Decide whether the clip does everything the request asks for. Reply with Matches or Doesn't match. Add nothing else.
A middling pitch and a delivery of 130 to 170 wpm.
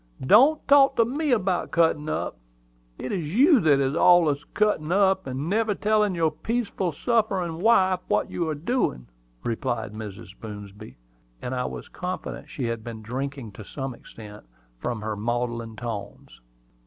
Matches